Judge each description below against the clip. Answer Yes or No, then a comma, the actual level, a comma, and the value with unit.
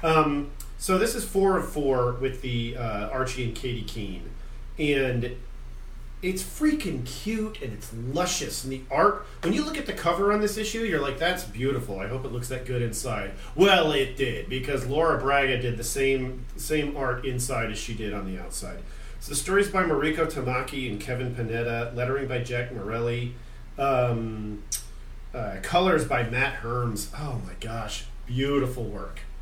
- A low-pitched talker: Yes, low, 125 Hz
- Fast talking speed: No, average, 175 wpm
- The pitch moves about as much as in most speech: Yes, average, 3.7 semitones